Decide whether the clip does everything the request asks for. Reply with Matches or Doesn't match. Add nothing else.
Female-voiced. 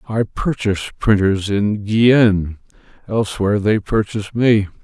Doesn't match